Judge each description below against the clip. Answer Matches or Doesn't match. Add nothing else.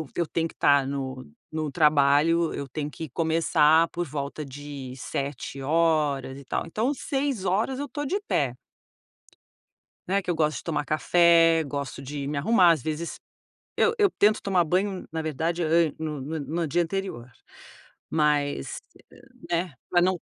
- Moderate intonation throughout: Matches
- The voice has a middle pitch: Matches